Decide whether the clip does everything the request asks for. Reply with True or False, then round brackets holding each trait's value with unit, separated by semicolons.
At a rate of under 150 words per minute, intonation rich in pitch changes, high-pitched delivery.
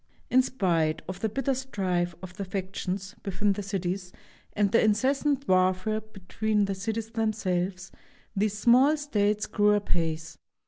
False (140 wpm; 3.0 semitones; 200 Hz)